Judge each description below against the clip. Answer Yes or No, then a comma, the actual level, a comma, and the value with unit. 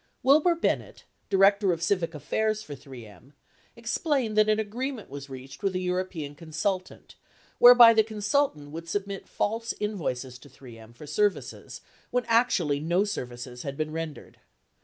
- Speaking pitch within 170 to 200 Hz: Yes, medium, 185 Hz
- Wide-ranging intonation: Yes, wide, 7.0 semitones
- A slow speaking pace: No, average, 155 wpm